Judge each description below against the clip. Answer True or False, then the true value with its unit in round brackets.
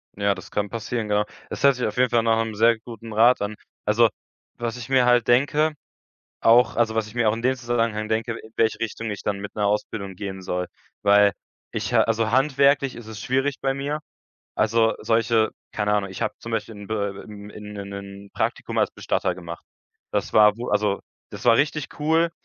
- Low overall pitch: True (115 Hz)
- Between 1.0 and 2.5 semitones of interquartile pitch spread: False (2.9 semitones)